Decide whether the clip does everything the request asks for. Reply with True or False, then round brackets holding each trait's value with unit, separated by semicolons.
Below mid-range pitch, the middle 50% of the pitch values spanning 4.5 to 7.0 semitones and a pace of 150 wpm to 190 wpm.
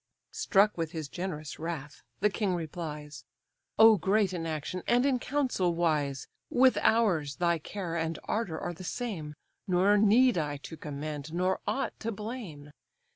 False (175 Hz; 5.4 semitones; 155 wpm)